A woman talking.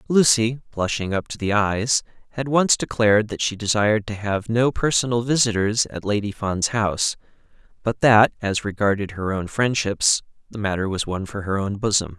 No: male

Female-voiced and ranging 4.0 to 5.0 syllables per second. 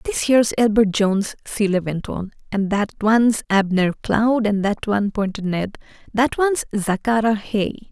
Yes: female; 4.8 syllables/s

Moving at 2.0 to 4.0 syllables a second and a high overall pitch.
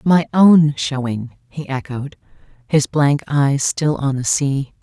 No: 3.5 syllables/s; medium, 140 Hz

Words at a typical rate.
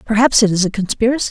No: fast, 230 wpm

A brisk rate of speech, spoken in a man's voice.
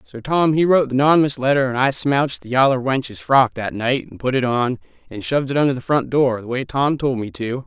Yes: fast, 260 wpm; male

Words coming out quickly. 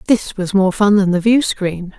Yes: fast, 210 wpm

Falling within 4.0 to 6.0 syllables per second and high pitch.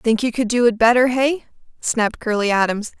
Yes: 5.5 syllables/s; high, 230 Hz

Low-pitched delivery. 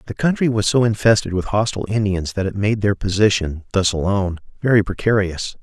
Yes: low, 100 Hz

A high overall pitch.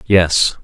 No: very low, 85 Hz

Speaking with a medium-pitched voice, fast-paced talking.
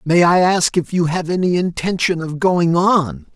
No: medium, 170 Hz; average, 195 wpm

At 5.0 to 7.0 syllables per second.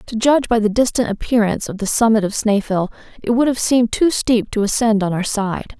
Yes: 5.8 syllables/s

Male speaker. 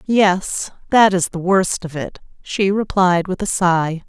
No: female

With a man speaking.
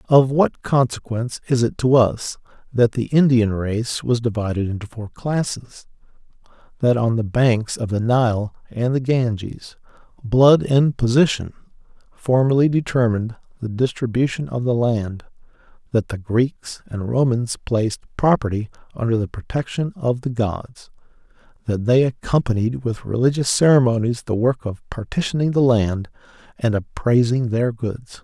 Yes: male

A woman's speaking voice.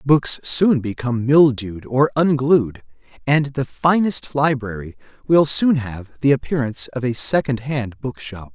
No: male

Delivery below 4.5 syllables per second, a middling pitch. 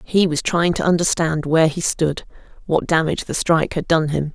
No: 5.5 syllables/s; medium, 165 Hz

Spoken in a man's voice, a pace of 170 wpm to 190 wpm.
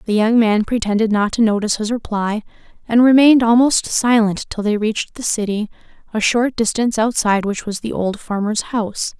No: female; average, 185 wpm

